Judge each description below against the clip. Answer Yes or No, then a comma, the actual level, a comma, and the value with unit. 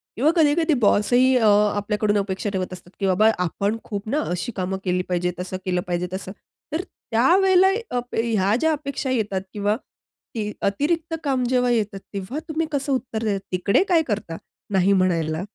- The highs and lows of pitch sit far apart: Yes, wide, 5.7 semitones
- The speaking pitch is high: Yes, high, 210 Hz